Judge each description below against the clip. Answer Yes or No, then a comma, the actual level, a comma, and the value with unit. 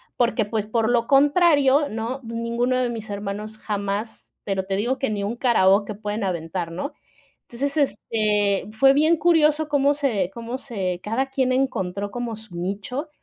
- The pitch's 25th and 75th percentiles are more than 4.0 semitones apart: Yes, average, 4.8 semitones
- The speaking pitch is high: Yes, high, 230 Hz